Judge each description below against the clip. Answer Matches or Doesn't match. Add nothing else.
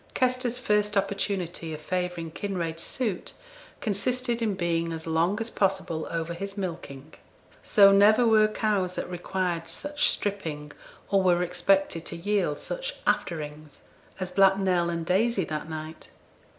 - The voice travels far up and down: Doesn't match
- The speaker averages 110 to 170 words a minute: Matches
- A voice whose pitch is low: Doesn't match